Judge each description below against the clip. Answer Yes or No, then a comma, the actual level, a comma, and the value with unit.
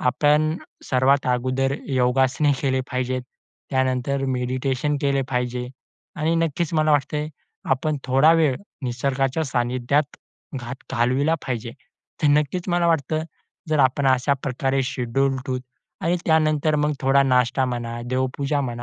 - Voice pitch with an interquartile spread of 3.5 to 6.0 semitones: No, narrow, 2.6 semitones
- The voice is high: No, low, 135 Hz